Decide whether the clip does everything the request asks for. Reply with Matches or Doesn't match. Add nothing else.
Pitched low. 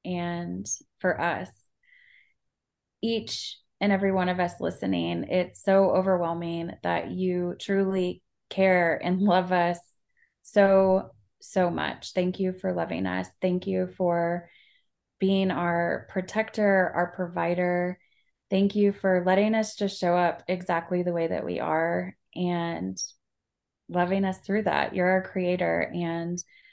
Doesn't match